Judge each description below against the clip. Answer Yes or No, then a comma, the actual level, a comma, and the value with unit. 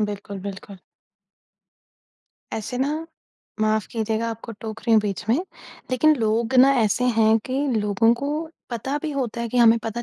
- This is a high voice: Yes, high, 230 Hz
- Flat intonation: No, average, 3.0 semitones